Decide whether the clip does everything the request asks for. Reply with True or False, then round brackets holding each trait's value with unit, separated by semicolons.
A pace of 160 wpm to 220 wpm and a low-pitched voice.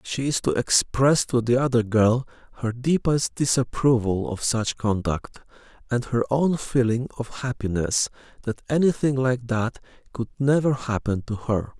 False (145 wpm; 120 Hz)